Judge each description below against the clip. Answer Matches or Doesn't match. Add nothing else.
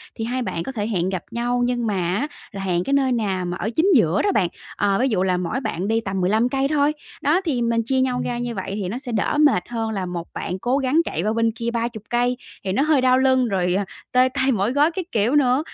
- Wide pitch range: Doesn't match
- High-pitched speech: Matches